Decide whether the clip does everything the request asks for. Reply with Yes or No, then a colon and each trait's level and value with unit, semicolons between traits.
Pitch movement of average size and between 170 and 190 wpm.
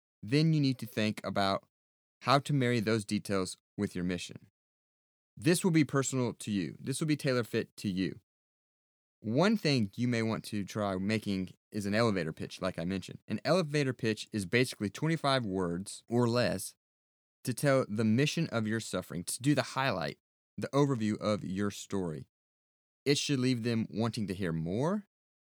No: wide, 5.7 semitones; average, 175 wpm